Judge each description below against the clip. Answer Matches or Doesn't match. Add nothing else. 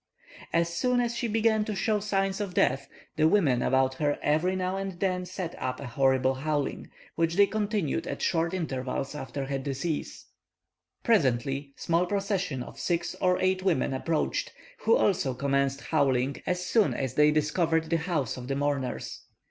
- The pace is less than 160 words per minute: Doesn't match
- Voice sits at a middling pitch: Matches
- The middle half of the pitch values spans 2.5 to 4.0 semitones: Doesn't match